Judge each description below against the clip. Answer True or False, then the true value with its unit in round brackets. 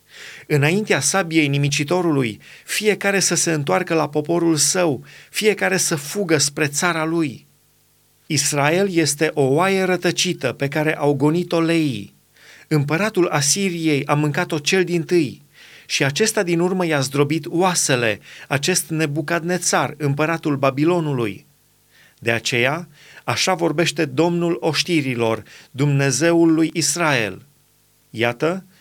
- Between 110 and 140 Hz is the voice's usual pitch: False (155 Hz)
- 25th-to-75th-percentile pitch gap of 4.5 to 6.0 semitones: False (3.2 semitones)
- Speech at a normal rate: False (110 wpm)